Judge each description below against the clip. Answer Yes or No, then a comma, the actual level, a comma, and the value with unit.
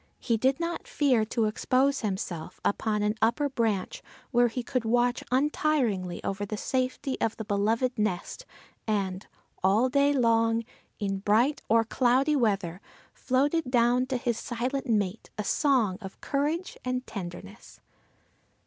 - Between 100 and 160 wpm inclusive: Yes, average, 140 wpm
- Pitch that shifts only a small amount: No, average, 3.9 semitones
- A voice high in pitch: Yes, high, 235 Hz